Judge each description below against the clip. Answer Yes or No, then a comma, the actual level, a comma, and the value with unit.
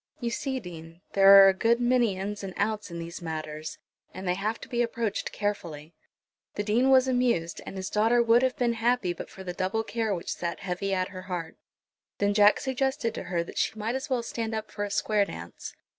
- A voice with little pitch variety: No, average, 4.3 semitones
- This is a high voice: Yes, high, 205 Hz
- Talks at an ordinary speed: No, fast, 220 wpm